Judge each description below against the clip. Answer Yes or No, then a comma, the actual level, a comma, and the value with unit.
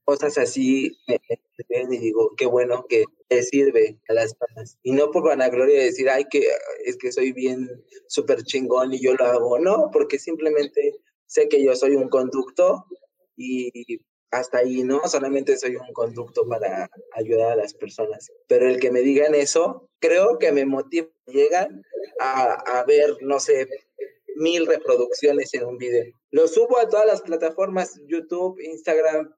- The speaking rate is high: No, average, 175 wpm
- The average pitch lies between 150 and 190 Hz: Yes, medium, 185 Hz